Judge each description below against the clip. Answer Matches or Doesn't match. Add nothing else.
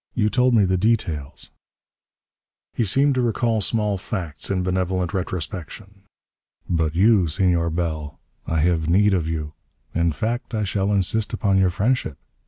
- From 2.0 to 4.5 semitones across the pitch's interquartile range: Matches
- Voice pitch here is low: Matches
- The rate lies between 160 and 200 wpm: Doesn't match